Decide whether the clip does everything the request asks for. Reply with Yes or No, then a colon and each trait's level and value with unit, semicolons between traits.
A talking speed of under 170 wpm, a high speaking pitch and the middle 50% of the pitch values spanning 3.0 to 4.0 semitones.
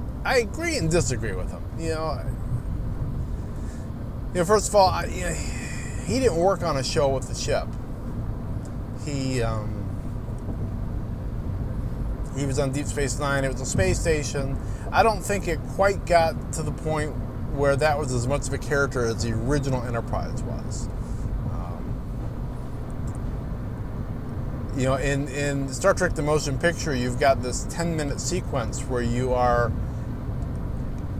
No: average, 155 wpm; low, 120 Hz; average, 3.3 semitones